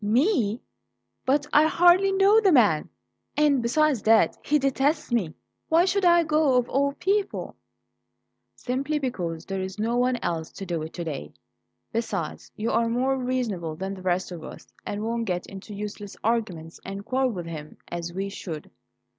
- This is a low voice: No, high, 230 Hz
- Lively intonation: Yes, wide, 6.9 semitones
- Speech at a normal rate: Yes, average, 170 wpm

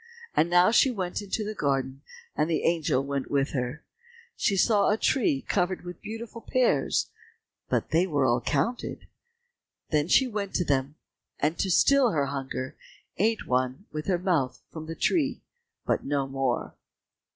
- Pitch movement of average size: No, wide, 6.8 semitones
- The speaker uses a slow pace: No, average, 160 wpm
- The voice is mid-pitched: Yes, medium, 165 Hz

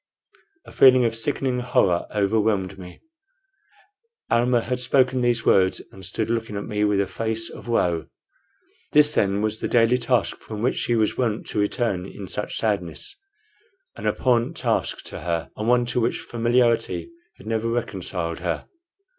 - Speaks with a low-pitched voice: Yes, low, 115 Hz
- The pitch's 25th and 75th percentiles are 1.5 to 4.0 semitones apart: Yes, average, 3.5 semitones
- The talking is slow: No, average, 165 wpm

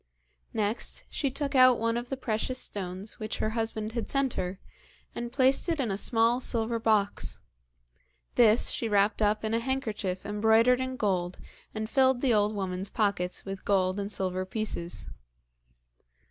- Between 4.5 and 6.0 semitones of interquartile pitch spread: No, average, 3.3 semitones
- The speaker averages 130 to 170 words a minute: Yes, average, 160 wpm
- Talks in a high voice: Yes, high, 220 Hz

